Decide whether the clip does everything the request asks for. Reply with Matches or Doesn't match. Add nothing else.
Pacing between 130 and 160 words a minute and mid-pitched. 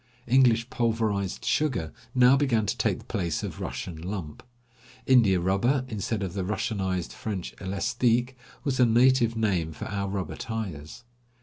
Doesn't match